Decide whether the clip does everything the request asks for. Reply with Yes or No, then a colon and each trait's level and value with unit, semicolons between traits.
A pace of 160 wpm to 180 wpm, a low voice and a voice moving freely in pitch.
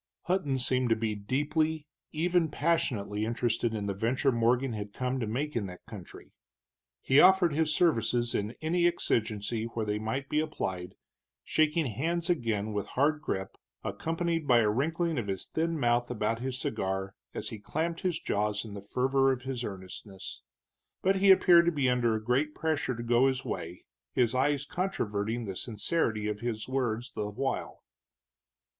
Yes: average, 170 wpm; low, 125 Hz; wide, 6.1 semitones